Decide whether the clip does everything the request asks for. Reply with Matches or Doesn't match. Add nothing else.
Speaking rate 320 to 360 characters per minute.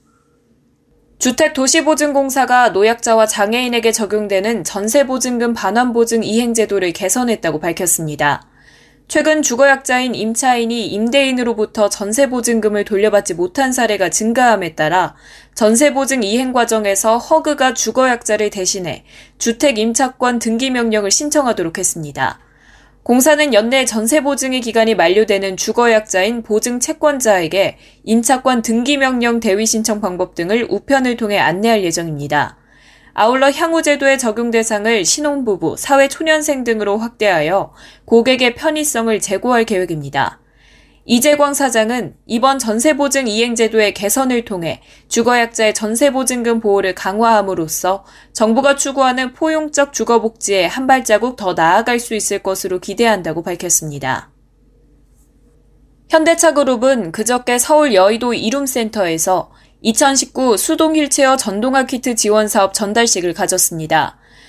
Matches